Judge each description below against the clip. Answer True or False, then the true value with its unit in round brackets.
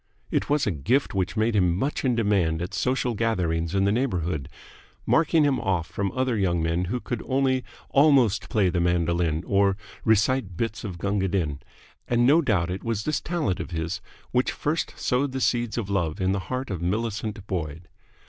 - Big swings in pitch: True (6.0 semitones)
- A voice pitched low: True (100 Hz)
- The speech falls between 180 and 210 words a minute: True (190 wpm)